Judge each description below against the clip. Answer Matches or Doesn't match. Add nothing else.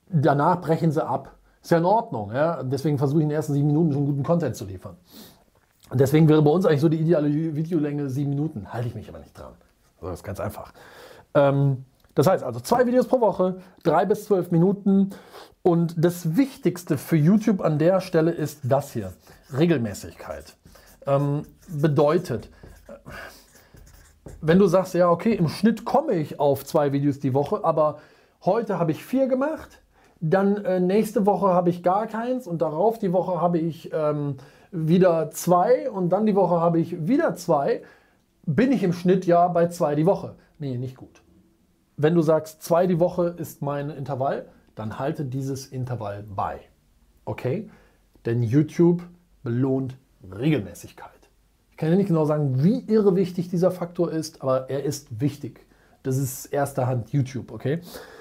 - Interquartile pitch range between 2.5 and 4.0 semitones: Doesn't match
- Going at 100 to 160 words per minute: Doesn't match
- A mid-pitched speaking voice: Matches